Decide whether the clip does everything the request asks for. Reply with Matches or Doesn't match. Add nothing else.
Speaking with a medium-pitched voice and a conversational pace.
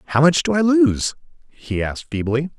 Matches